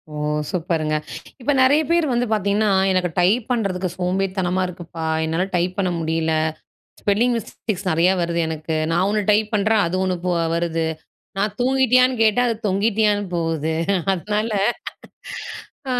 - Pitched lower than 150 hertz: No, high, 190 Hz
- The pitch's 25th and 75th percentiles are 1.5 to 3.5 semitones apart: No, average, 4.2 semitones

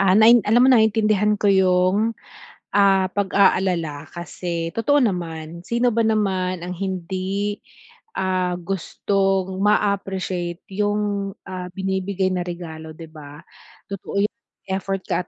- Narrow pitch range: Yes, narrow, 2.3 semitones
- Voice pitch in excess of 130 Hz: Yes, high, 190 Hz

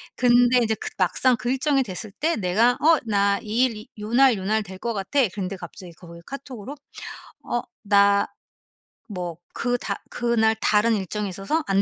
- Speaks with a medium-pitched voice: No, high, 215 Hz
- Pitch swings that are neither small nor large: Yes, average, 3.9 semitones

